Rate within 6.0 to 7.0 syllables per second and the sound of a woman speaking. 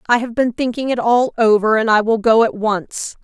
No: 5.0 syllables/s; female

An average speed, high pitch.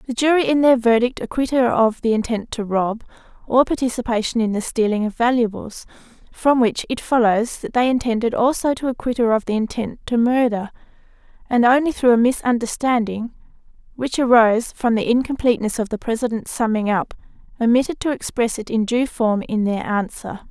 Yes: average, 175 wpm; high, 235 Hz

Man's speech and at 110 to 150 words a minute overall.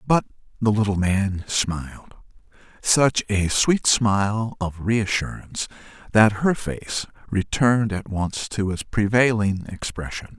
Yes: male; slow, 135 wpm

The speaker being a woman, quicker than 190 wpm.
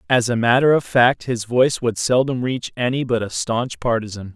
No: male; fast, 205 wpm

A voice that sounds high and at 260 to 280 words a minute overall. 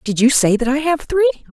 Yes: very high, 270 Hz; fast, 270 wpm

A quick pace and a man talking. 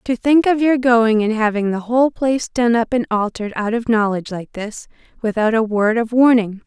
No: fast, 215 wpm; female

